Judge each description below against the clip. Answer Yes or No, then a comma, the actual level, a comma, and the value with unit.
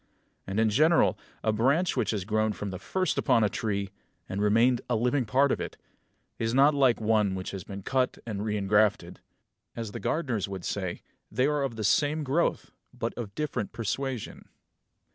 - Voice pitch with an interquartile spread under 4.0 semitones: No, average, 4.5 semitones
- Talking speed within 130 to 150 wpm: No, average, 180 wpm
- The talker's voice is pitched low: Yes, low, 110 Hz